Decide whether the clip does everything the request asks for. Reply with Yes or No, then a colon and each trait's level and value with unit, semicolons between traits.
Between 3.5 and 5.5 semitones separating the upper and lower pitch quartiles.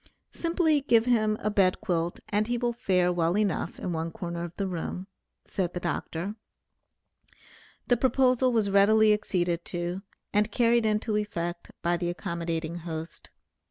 Yes: average, 4.0 semitones